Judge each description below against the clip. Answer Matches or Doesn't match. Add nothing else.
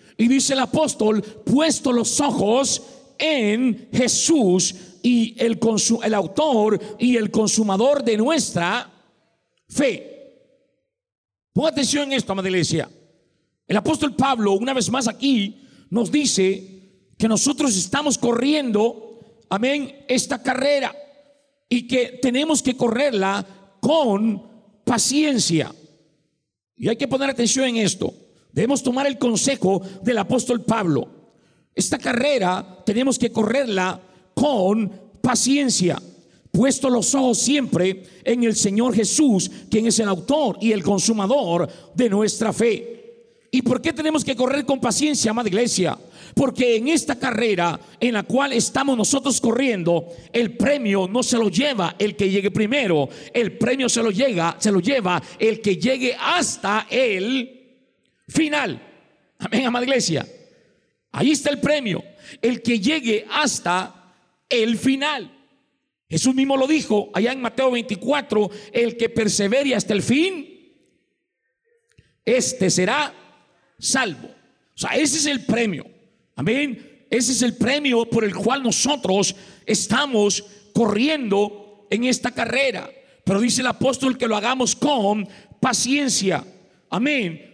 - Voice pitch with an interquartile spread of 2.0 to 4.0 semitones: Doesn't match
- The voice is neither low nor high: Doesn't match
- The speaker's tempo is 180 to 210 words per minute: Doesn't match